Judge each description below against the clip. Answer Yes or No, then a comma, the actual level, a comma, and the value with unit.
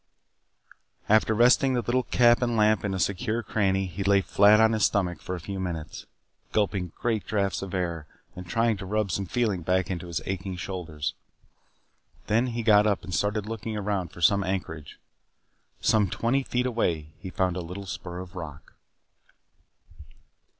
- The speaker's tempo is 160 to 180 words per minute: Yes, average, 170 wpm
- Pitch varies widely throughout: No, average, 3.2 semitones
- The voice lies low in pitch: Yes, low, 100 Hz